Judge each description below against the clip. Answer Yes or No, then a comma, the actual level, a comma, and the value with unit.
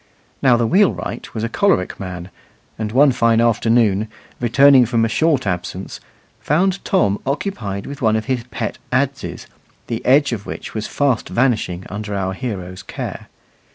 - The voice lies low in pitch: Yes, low, 115 Hz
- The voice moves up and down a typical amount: Yes, average, 4.8 semitones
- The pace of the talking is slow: No, average, 155 wpm